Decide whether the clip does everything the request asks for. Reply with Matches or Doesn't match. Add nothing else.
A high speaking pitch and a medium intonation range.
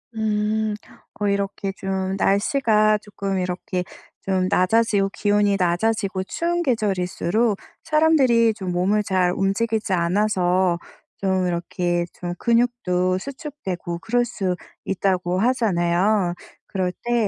Matches